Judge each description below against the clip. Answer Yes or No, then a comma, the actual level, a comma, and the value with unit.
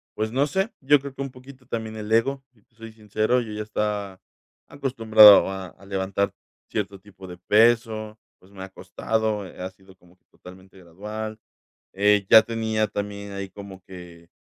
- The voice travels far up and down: No, average, 2.8 semitones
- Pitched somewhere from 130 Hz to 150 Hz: No, low, 105 Hz